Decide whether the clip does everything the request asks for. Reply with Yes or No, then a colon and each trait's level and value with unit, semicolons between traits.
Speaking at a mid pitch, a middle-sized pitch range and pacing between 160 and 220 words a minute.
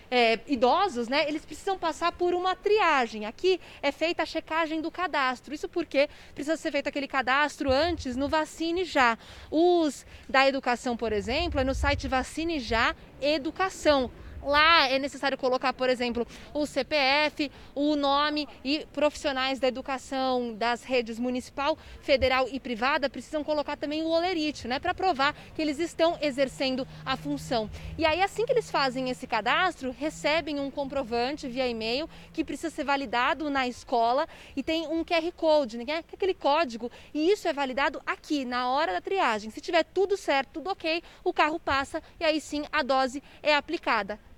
No: very high, 295 Hz; average, 3.7 semitones; average, 170 wpm